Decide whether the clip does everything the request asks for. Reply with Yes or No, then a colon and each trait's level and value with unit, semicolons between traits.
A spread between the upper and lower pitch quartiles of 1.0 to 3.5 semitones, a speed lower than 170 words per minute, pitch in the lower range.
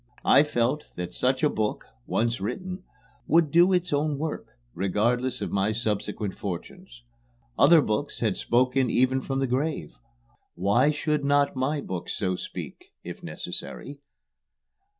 No: wide, 5.6 semitones; average, 140 wpm; low, 130 Hz